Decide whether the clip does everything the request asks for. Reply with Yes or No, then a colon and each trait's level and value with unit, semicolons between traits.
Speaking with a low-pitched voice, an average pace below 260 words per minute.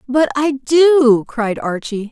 No: very high, 260 Hz; average, 140 wpm